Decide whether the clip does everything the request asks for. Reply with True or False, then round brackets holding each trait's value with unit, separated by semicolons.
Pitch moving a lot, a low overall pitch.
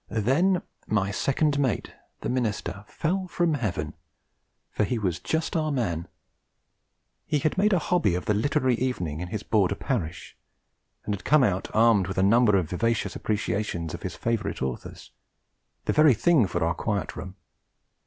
True (7.1 semitones; 110 Hz)